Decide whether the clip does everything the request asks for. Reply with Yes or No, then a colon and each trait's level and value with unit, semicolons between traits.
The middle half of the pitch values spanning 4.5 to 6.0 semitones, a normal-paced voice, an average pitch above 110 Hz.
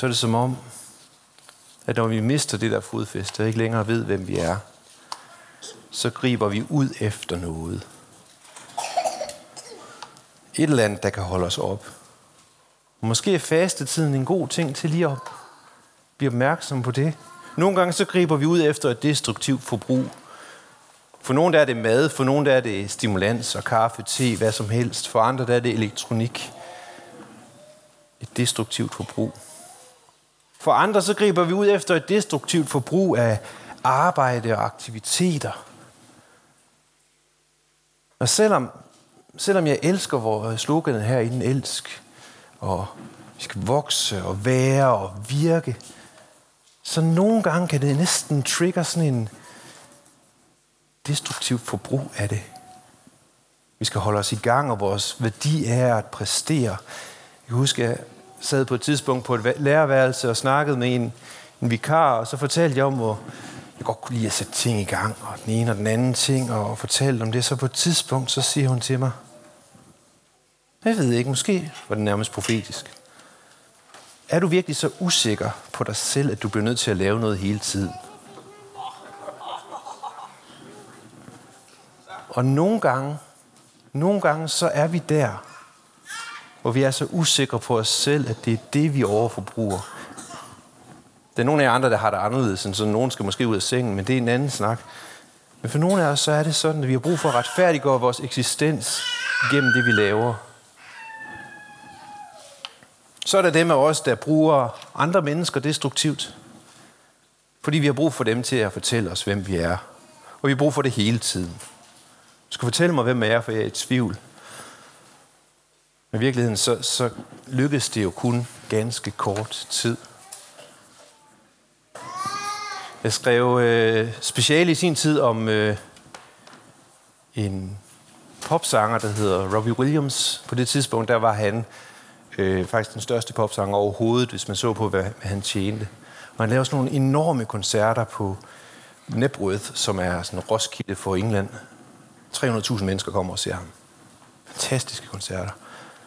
Yes: average, 5.2 semitones; average, 165 wpm; low, 125 Hz